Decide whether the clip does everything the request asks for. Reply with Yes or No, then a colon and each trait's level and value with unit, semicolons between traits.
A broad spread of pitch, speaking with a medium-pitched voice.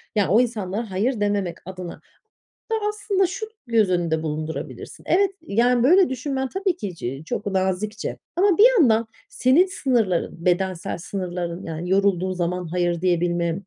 No: wide, 6.5 semitones; high, 200 Hz